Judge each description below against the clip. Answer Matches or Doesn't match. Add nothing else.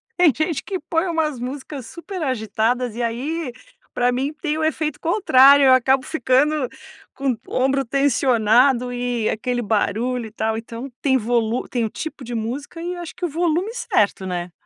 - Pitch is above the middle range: Matches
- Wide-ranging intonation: Doesn't match